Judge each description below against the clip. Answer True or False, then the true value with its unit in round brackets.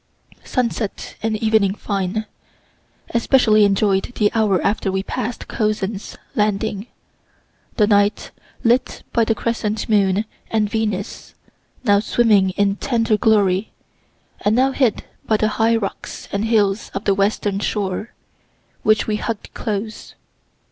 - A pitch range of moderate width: False (2.0 semitones)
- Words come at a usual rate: False (125 wpm)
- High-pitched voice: True (215 Hz)